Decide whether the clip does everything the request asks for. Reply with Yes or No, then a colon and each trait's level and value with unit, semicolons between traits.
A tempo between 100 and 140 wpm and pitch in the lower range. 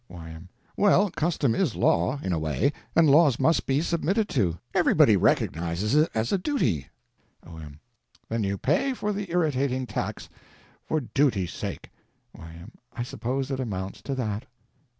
No: average, 150 wpm; low, 130 Hz